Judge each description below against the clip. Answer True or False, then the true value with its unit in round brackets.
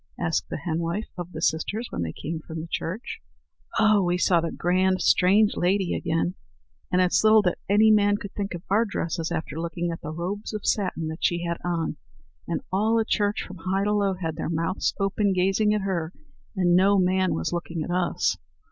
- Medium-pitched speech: True (180 Hz)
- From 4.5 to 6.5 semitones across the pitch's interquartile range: False (3.3 semitones)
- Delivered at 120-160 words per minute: False (205 wpm)